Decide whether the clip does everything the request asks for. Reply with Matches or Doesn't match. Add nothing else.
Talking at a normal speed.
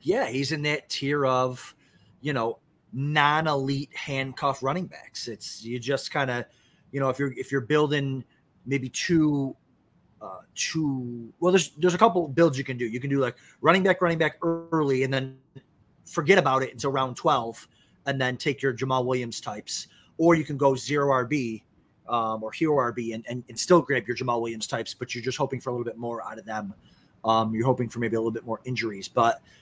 Doesn't match